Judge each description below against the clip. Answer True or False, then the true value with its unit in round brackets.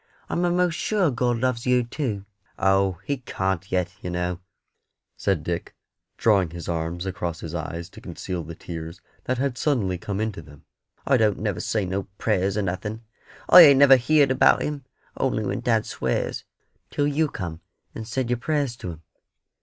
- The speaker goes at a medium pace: True (175 wpm)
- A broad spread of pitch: True (6.5 semitones)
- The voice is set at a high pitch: False (105 Hz)